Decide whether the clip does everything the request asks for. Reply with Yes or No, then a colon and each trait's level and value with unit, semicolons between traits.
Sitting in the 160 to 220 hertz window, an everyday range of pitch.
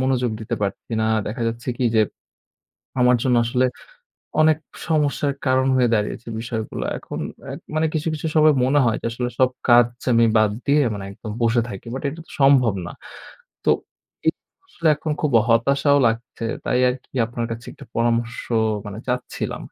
No: low, 125 Hz; average, 3.2 semitones